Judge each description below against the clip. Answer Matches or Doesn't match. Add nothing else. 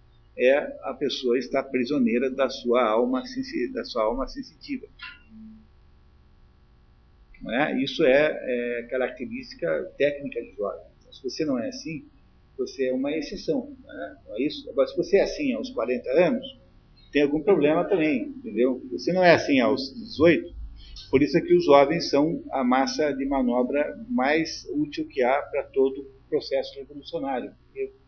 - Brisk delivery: Doesn't match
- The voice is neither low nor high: Matches